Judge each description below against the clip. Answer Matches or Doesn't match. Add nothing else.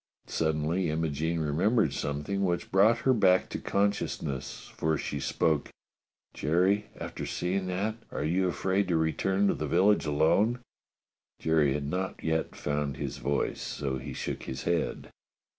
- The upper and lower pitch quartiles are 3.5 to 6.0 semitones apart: Matches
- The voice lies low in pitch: Matches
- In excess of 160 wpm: Doesn't match